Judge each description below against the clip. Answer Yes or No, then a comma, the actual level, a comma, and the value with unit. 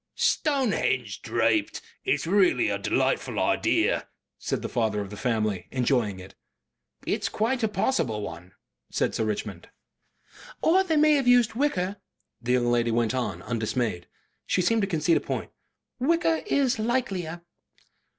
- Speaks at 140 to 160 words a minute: Yes, average, 145 wpm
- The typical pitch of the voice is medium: Yes, medium, 170 Hz